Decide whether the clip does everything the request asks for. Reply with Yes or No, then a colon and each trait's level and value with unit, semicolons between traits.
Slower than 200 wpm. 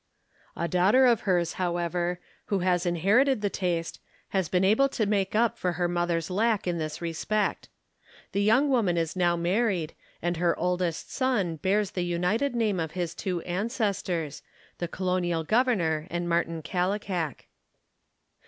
Yes: average, 155 wpm